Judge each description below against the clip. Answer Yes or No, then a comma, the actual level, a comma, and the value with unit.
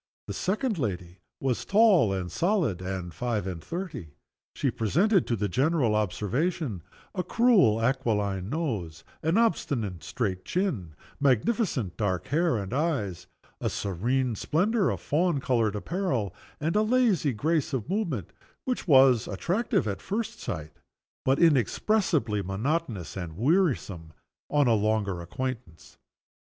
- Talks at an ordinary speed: No, slow, 130 wpm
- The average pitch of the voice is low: Yes, low, 130 Hz